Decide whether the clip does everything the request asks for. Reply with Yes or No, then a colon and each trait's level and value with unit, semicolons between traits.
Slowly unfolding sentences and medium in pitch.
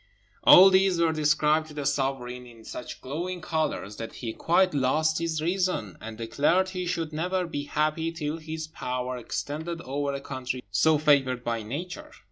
No: average, 170 wpm; medium, 150 Hz